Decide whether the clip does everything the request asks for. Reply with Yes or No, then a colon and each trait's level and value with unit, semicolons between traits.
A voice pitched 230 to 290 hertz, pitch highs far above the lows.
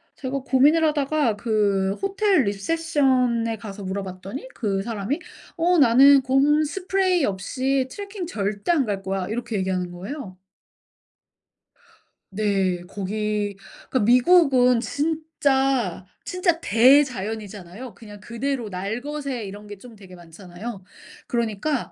Yes: high, 235 Hz; wide, 6.1 semitones